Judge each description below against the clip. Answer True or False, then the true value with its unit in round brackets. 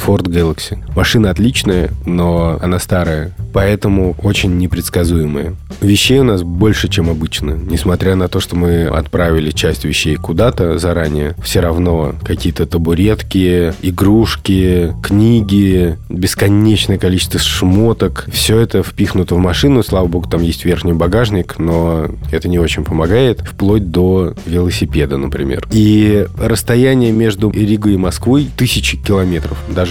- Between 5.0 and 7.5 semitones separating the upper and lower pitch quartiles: False (3.4 semitones)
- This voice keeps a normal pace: True (130 wpm)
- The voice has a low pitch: True (90 Hz)